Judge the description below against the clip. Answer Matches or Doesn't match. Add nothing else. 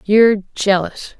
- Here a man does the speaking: Doesn't match